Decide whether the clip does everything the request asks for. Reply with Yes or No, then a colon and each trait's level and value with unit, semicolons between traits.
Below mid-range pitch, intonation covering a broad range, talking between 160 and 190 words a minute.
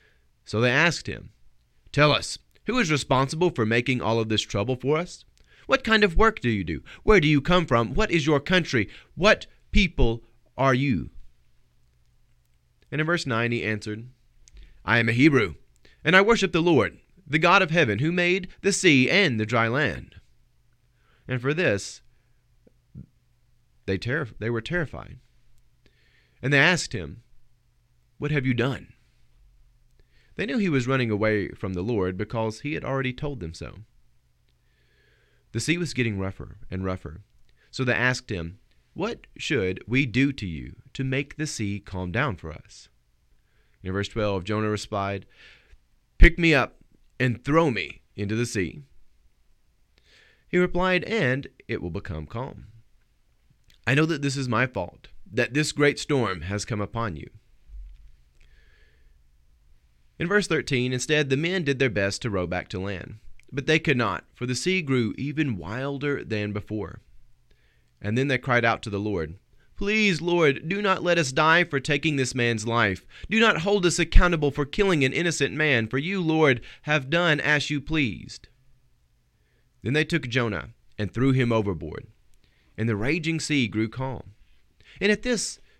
Yes: low, 120 Hz; wide, 6.9 semitones; average, 165 wpm